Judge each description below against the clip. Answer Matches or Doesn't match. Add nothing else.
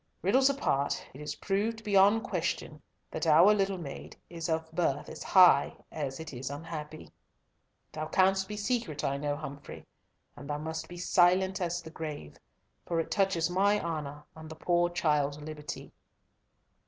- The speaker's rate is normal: Matches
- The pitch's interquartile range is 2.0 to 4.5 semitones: Matches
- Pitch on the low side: Doesn't match